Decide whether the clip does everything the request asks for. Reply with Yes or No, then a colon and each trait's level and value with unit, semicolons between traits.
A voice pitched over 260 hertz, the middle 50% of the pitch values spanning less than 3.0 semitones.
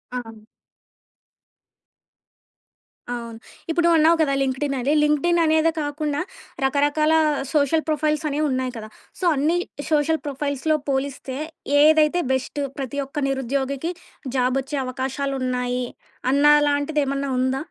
Yes: very high, 280 Hz; narrow, 2.6 semitones